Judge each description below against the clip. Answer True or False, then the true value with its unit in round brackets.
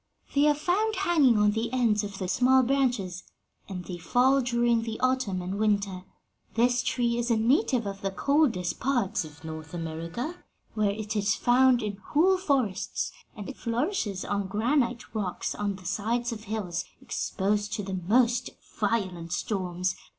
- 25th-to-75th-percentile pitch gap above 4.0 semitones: True (4.5 semitones)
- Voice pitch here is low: False (220 Hz)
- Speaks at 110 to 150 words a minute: False (165 wpm)